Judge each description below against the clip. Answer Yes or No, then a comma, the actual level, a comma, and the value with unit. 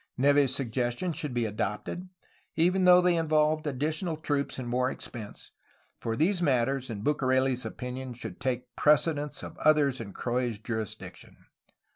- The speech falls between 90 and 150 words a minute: Yes, average, 145 wpm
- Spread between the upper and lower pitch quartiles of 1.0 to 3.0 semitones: No, average, 4.1 semitones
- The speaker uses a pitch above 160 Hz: No, low, 135 Hz